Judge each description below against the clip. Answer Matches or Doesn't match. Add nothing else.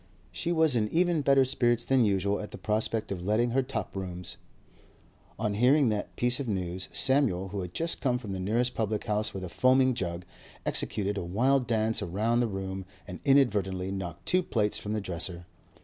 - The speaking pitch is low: Matches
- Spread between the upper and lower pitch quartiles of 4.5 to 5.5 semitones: Matches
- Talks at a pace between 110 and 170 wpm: Doesn't match